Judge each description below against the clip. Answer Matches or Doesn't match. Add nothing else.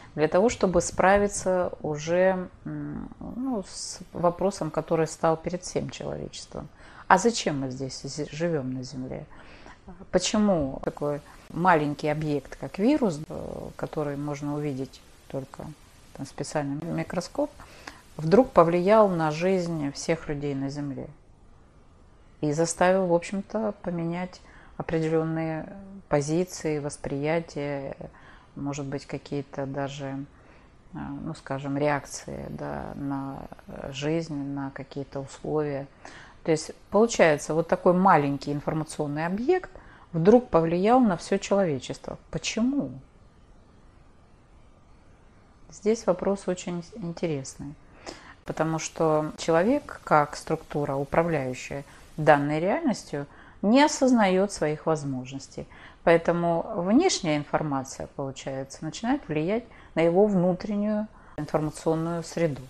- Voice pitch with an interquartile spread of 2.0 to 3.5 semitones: Doesn't match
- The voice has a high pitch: Doesn't match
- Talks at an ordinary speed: Doesn't match